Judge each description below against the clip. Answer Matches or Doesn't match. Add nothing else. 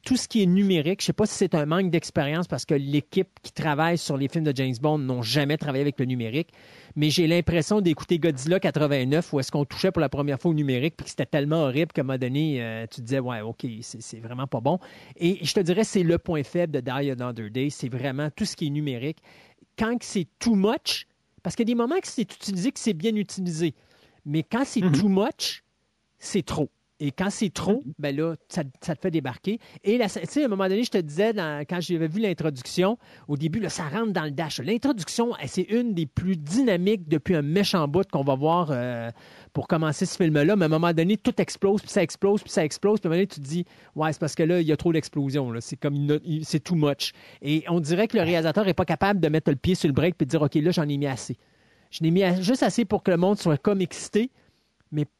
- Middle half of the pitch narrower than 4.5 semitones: Doesn't match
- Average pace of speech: Doesn't match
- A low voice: Doesn't match